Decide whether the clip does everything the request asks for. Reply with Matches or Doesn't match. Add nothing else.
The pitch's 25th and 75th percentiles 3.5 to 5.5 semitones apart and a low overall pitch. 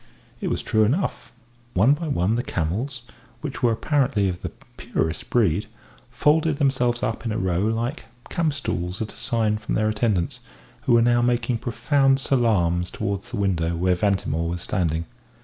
Matches